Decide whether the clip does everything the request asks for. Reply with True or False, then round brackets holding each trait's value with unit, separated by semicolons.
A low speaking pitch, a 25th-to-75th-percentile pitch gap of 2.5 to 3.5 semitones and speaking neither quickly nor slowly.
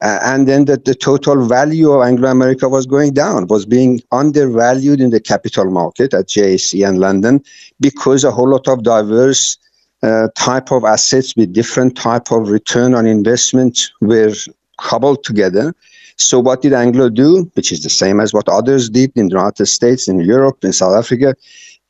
True (125 Hz; 3.2 semitones; 180 wpm)